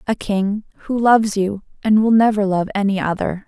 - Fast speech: No, average, 190 wpm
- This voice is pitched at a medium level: No, high, 205 Hz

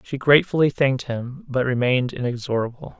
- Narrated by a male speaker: Yes, male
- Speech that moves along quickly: No, average, 140 wpm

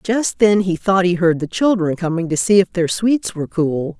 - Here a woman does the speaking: Yes, female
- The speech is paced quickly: Yes, fast, 240 wpm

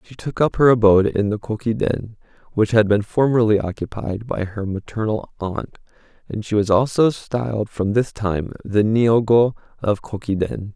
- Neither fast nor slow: Yes, average, 160 wpm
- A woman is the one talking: No, male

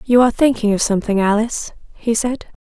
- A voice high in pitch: Yes, high, 225 Hz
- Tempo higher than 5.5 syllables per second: Yes, 6.2 syllables/s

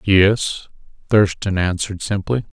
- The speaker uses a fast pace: No, slow, 95 wpm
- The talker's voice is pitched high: No, low, 100 Hz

